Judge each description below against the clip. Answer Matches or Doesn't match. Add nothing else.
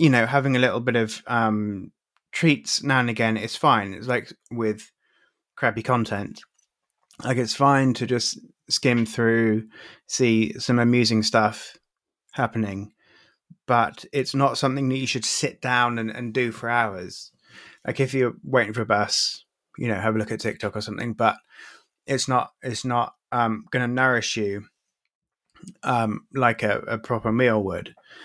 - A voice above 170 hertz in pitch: Doesn't match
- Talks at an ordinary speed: Matches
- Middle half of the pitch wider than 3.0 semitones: Doesn't match